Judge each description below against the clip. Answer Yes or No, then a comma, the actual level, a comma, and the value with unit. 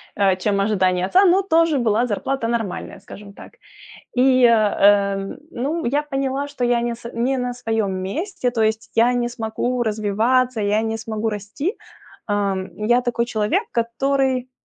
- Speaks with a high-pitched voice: Yes, high, 235 Hz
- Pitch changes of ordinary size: Yes, average, 3.5 semitones